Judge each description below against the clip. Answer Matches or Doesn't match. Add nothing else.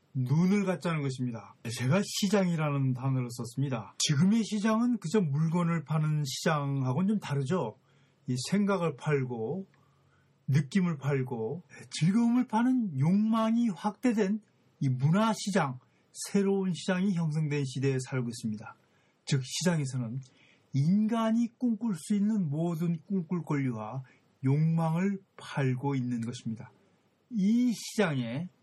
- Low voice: Doesn't match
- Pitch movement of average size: Doesn't match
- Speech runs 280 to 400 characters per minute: Doesn't match